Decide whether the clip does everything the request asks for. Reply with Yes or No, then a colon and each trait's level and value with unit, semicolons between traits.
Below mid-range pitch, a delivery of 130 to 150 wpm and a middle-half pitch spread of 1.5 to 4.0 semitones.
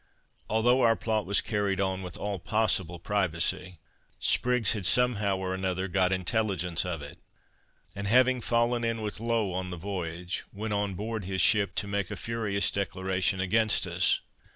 No: low, 100 Hz; average, 165 wpm; average, 3.2 semitones